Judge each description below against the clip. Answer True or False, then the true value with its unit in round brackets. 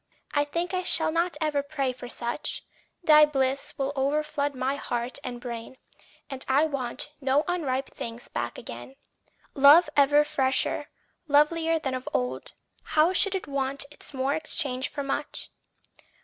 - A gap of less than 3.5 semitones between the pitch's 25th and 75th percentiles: True (2.7 semitones)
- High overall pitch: True (280 Hz)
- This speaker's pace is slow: False (150 wpm)